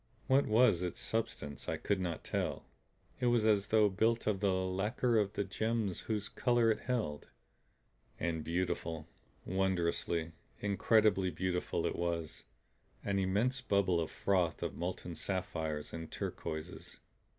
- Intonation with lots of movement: No, average, 4.2 semitones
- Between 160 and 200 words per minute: No, average, 140 wpm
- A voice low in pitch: Yes, very low, 95 Hz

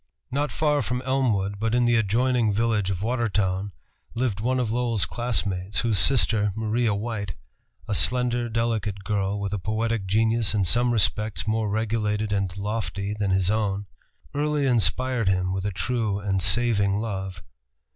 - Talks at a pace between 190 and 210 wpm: No, average, 155 wpm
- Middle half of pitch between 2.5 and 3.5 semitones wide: Yes, average, 3.0 semitones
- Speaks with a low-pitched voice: Yes, low, 110 Hz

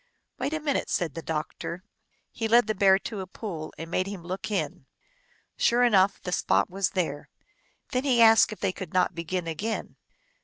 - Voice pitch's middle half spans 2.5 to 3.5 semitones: No, average, 4.4 semitones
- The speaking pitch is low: No, high, 190 Hz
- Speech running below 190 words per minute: No, average, 195 wpm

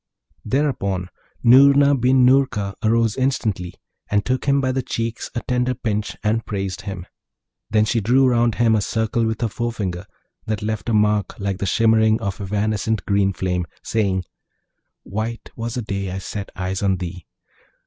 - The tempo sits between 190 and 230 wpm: No, average, 165 wpm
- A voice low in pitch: Yes, low, 110 Hz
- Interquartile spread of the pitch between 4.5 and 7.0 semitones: No, average, 3.3 semitones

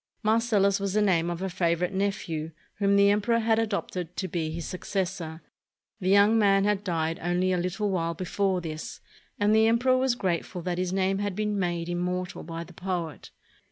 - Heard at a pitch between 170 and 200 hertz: Yes, medium, 185 Hz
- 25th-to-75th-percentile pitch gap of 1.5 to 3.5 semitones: Yes, average, 2.8 semitones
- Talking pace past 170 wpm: Yes, average, 195 wpm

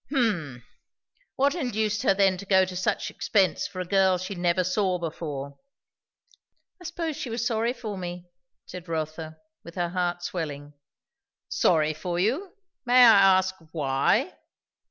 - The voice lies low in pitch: No, medium, 185 Hz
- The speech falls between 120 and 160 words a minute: Yes, average, 150 wpm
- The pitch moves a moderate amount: Yes, average, 4.2 semitones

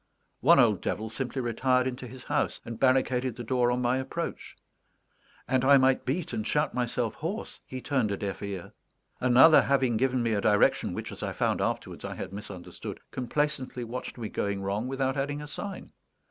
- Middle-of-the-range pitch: No, low, 125 Hz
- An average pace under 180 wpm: No, average, 190 wpm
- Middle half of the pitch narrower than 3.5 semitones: Yes, average, 2.7 semitones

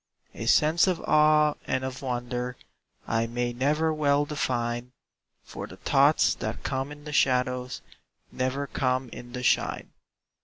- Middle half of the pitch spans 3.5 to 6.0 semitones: No, average, 3.1 semitones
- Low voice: Yes, low, 130 Hz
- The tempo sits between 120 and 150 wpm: Yes, average, 145 wpm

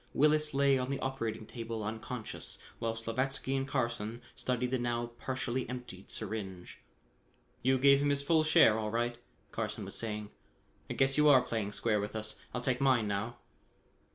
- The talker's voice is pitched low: Yes, low, 120 Hz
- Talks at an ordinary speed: Yes, average, 170 wpm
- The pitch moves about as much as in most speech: Yes, average, 3.3 semitones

